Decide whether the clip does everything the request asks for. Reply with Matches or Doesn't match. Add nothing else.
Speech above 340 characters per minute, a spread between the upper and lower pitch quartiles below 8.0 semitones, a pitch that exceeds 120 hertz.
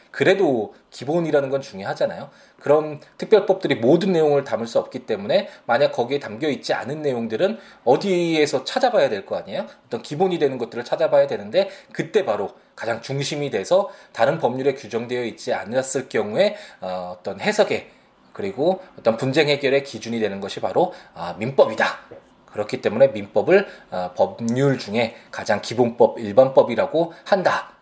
Matches